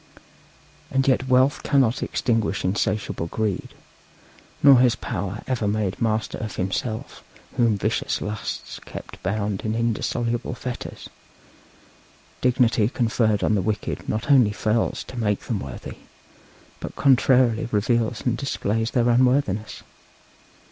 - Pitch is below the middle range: Yes, low, 115 Hz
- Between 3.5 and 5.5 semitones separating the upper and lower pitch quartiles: No, average, 3.0 semitones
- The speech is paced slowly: Yes, slow, 125 wpm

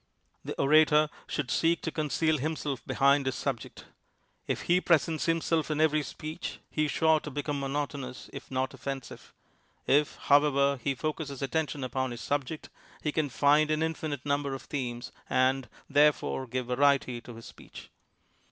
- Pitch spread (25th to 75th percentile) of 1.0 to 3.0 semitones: Yes, narrow, 2.5 semitones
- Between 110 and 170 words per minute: Yes, average, 160 wpm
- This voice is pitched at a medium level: Yes, medium, 145 Hz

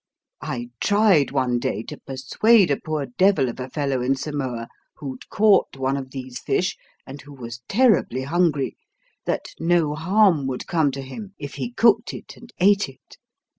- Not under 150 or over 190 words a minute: Yes, average, 170 wpm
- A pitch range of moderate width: No, wide, 6.3 semitones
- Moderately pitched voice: Yes, medium, 145 Hz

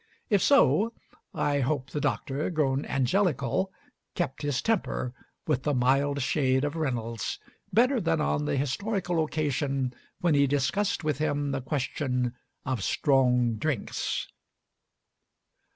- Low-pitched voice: No, medium, 145 Hz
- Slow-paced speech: Yes, slow, 125 wpm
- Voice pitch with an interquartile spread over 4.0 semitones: No, average, 3.2 semitones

